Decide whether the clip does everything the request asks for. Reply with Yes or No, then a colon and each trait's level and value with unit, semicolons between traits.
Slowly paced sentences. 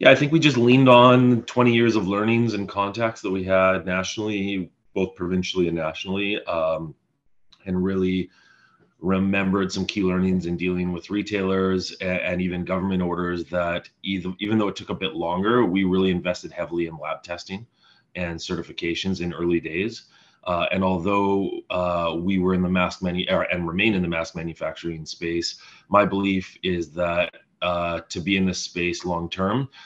No: average, 175 wpm